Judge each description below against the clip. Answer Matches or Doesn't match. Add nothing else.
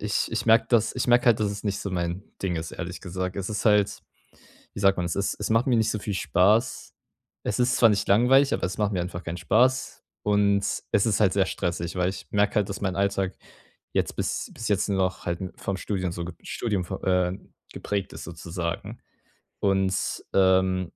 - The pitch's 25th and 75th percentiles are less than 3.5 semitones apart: Matches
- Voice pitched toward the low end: Matches